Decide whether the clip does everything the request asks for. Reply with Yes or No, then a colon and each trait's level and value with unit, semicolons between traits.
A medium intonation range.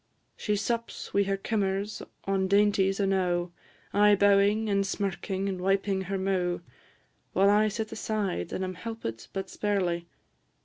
No: narrow, 1.5 semitones